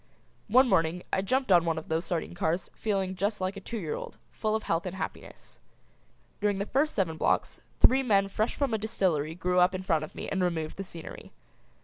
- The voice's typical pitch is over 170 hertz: Yes, high, 190 Hz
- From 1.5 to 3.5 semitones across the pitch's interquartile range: No, average, 4.1 semitones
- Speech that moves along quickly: Yes, fast, 220 wpm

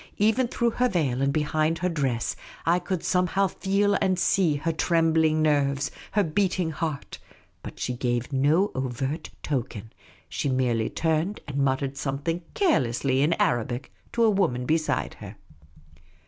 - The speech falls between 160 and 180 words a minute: No, average, 150 wpm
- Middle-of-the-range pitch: Yes, medium, 155 Hz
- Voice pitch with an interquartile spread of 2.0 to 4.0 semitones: No, average, 5.2 semitones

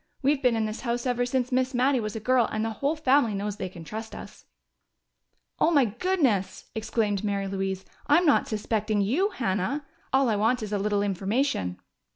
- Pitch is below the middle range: No, high, 225 Hz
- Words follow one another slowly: No, average, 195 wpm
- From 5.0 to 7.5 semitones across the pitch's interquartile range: No, average, 4.3 semitones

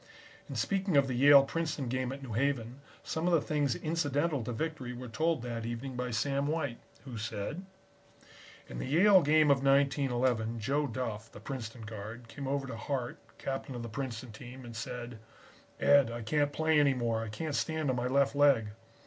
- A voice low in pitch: Yes, low, 130 Hz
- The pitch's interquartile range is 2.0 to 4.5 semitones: Yes, average, 3.5 semitones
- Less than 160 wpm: No, average, 190 wpm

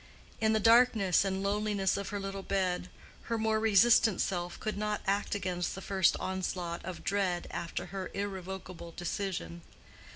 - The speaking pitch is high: Yes, high, 195 Hz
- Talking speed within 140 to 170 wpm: Yes, average, 155 wpm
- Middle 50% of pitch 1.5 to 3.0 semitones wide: Yes, narrow, 2.4 semitones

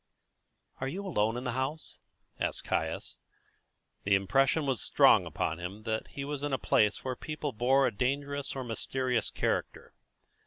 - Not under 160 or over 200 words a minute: Yes, average, 165 wpm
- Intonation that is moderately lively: Yes, average, 4.1 semitones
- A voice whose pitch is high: No, low, 130 Hz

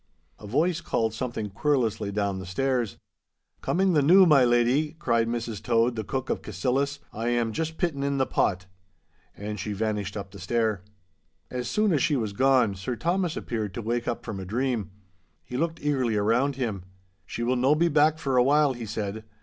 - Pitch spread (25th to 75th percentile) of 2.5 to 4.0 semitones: No, average, 4.7 semitones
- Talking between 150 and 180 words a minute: No, average, 195 wpm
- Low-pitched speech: Yes, low, 120 Hz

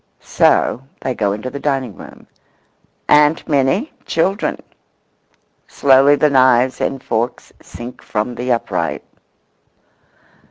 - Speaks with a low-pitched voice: Yes, low, 130 Hz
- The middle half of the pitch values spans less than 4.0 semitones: Yes, average, 2.9 semitones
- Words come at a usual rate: No, slow, 105 wpm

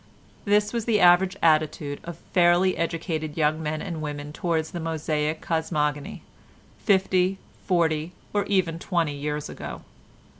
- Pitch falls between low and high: Yes, medium, 165 Hz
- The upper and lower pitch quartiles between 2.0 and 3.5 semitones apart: Yes, average, 2.9 semitones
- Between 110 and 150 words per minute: Yes, slow, 135 wpm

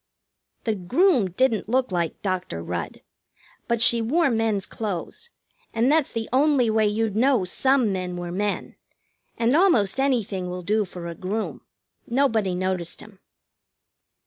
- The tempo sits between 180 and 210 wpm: No, average, 145 wpm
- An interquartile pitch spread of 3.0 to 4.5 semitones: No, wide, 5.4 semitones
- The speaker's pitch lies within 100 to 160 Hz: No, high, 220 Hz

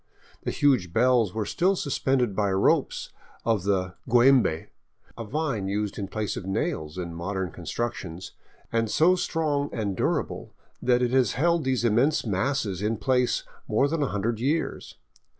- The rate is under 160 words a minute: Yes, average, 150 wpm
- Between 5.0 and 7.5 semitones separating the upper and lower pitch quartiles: Yes, average, 5.3 semitones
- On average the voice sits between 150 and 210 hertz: No, low, 115 Hz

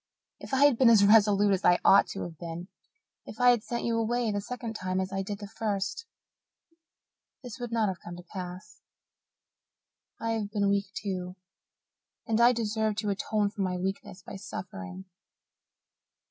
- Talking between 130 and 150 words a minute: No, average, 175 wpm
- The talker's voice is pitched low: No, high, 205 Hz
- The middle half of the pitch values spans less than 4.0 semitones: Yes, average, 3.1 semitones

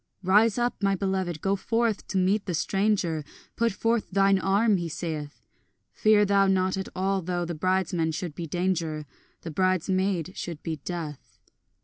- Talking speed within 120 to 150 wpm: No, average, 160 wpm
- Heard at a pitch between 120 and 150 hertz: No, medium, 185 Hz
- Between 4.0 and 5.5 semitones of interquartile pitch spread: No, average, 2.9 semitones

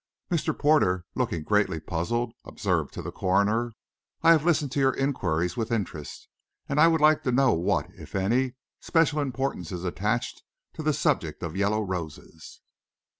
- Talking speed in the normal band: Yes, average, 165 wpm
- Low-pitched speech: Yes, low, 115 Hz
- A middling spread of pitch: No, wide, 7.1 semitones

